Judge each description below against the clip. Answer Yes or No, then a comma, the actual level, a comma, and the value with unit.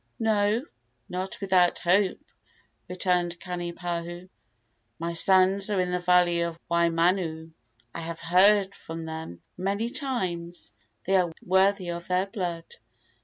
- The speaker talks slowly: Yes, slow, 120 wpm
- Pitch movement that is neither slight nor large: No, narrow, 2.0 semitones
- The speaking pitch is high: No, medium, 180 Hz